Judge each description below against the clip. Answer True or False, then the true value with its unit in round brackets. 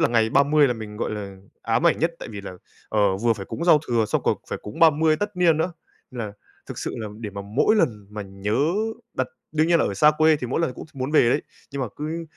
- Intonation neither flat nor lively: False (7.1 semitones)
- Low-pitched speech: True (125 Hz)